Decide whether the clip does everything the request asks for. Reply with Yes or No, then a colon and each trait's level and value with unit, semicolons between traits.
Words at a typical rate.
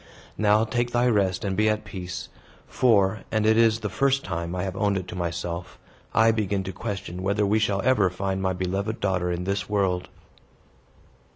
Yes: average, 190 wpm